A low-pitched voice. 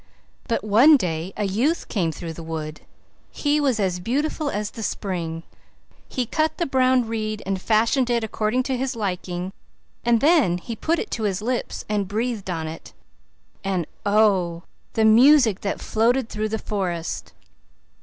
No: high, 215 Hz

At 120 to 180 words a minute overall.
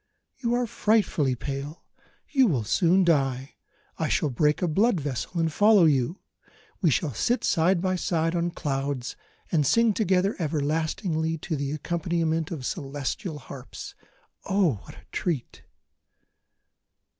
Yes: slow, 135 wpm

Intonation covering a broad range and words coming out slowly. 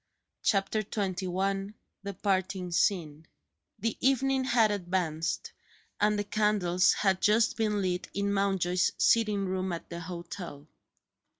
No: average, 2.8 semitones; slow, 120 wpm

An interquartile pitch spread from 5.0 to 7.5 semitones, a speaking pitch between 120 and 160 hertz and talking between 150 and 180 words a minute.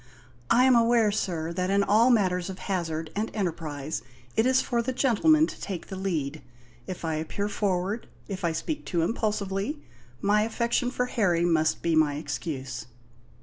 No: wide, 5.6 semitones; high, 195 Hz; average, 170 wpm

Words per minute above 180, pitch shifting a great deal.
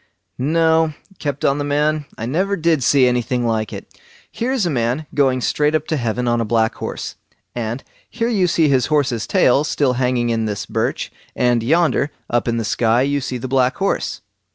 No: average, 195 wpm; average, 4.4 semitones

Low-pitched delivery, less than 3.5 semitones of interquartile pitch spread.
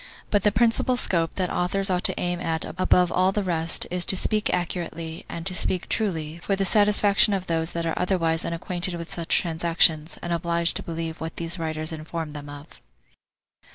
No: medium, 170 Hz; narrow, 2.4 semitones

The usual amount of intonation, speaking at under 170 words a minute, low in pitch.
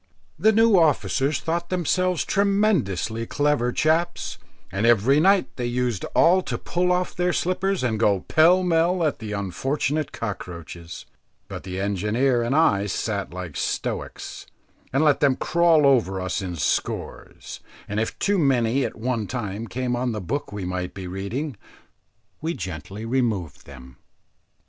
No: wide, 8.5 semitones; average, 150 wpm; low, 125 Hz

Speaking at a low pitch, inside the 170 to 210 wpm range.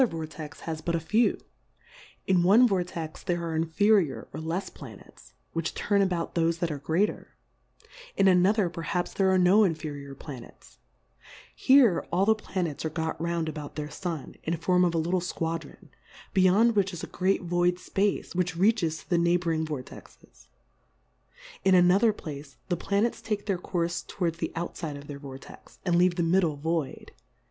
No: medium, 170 Hz; average, 175 wpm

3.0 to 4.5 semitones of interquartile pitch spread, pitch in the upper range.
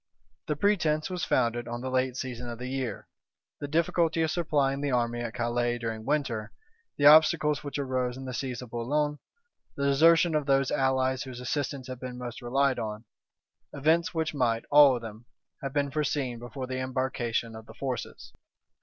No: average, 3.4 semitones; low, 130 Hz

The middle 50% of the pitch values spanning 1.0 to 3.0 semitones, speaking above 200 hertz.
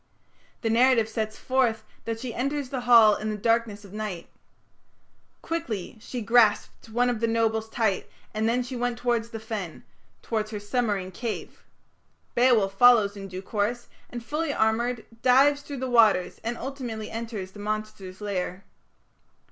Yes: narrow, 2.5 semitones; high, 225 Hz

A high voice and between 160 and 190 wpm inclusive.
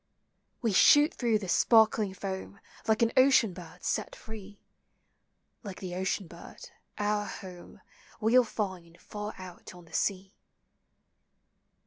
No: high, 200 Hz; slow, 135 wpm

